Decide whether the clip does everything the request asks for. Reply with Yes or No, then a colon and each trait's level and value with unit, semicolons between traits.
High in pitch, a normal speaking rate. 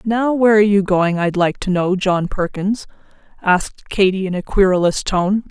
Yes: high, 195 Hz; average, 185 wpm